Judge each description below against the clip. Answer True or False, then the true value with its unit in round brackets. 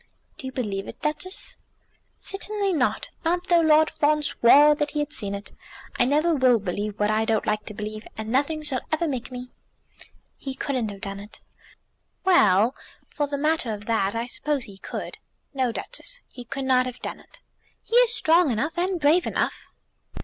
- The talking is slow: False (185 wpm)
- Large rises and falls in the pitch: True (6.1 semitones)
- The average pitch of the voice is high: True (265 Hz)